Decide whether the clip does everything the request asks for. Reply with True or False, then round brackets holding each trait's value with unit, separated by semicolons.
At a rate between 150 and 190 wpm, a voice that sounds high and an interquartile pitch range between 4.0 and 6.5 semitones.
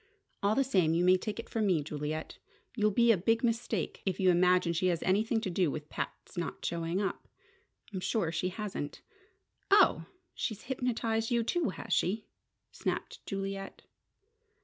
True (170 wpm; 195 Hz; 4.5 semitones)